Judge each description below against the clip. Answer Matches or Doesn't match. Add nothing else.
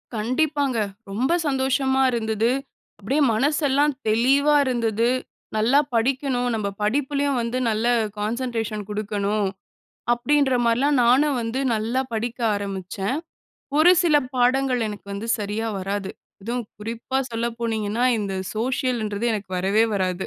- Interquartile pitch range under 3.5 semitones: Doesn't match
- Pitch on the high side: Matches